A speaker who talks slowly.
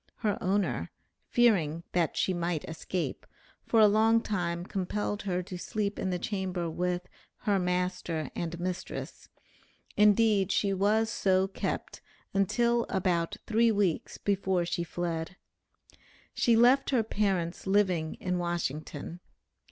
Yes: slow, 130 wpm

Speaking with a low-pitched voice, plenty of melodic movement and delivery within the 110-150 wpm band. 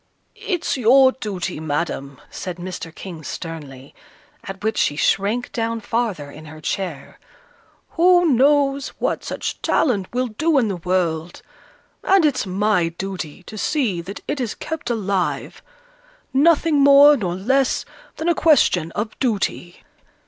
No: high, 210 Hz; wide, 7.7 semitones; average, 140 wpm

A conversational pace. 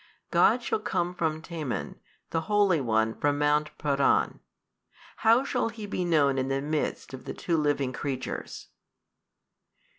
Yes: average, 145 wpm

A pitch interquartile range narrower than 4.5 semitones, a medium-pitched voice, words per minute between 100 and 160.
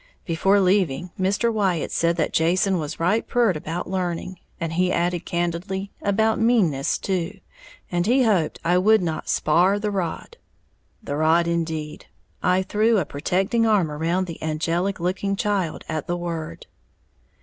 Yes: average, 3.1 semitones; medium, 180 Hz; average, 150 wpm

